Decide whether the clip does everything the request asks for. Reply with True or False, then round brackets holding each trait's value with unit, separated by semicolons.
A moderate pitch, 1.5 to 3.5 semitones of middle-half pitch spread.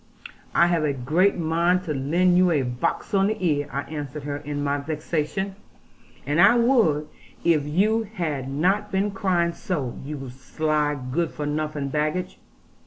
False (155 Hz; 4.0 semitones)